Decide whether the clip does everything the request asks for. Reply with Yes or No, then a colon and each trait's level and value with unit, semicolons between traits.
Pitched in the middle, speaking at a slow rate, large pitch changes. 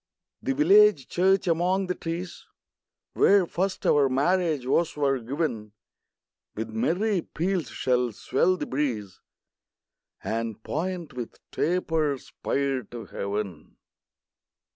Yes: medium, 150 Hz; slow, 110 wpm; wide, 6.9 semitones